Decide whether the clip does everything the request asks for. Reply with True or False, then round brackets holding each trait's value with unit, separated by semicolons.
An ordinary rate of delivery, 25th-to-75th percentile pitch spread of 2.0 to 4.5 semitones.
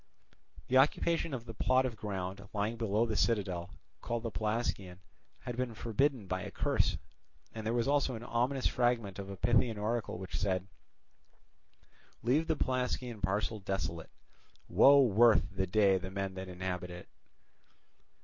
True (150 wpm; 4.1 semitones)